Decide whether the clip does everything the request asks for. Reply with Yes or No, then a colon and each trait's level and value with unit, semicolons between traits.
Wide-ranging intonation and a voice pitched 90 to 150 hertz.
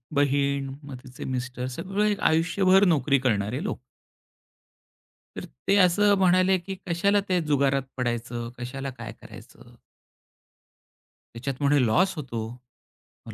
Yes: wide, 6.4 semitones; medium, 140 Hz